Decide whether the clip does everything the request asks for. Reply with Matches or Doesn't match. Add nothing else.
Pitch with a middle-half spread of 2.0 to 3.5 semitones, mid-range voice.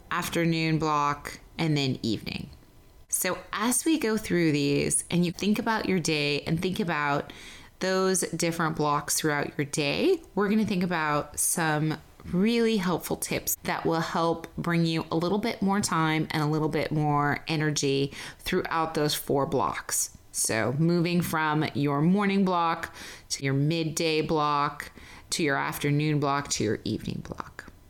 Matches